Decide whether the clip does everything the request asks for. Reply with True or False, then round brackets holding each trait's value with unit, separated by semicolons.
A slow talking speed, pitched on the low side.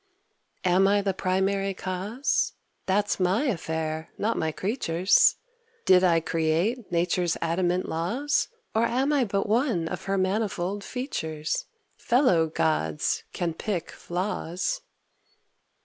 False (115 wpm; 185 Hz)